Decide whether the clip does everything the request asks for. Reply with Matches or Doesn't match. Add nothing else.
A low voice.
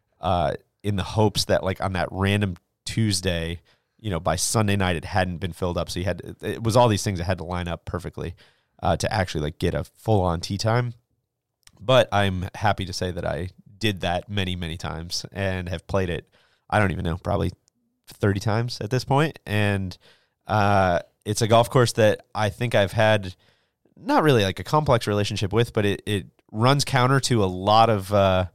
Matches